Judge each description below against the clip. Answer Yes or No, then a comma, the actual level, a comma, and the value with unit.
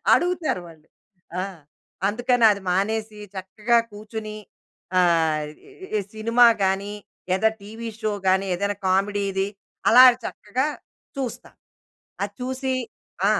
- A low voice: No, high, 210 Hz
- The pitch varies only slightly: No, average, 3.2 semitones